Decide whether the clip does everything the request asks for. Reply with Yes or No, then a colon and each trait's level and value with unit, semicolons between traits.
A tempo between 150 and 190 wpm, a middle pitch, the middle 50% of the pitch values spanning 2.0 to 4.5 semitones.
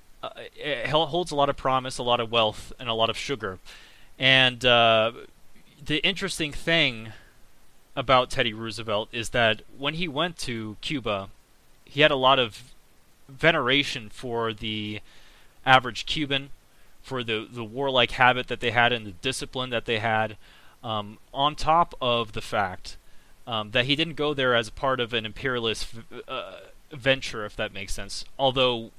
No: average, 165 wpm; low, 125 Hz; average, 3.7 semitones